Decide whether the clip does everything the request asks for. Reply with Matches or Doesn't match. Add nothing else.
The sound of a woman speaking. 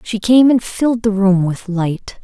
Matches